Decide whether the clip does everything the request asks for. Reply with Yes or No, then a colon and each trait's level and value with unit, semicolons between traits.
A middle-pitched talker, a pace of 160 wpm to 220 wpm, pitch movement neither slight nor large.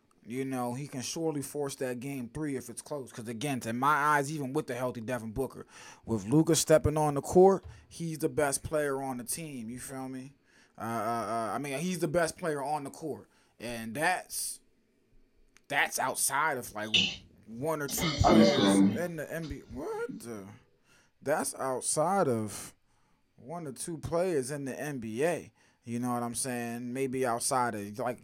No: low, 130 Hz; average, 180 wpm; average, 4.1 semitones